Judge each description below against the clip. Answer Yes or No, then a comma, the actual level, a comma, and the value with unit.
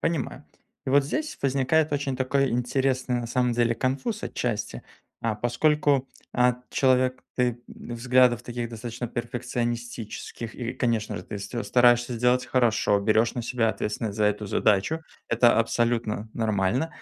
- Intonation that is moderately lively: No, narrow, 2.0 semitones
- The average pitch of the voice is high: No, low, 120 Hz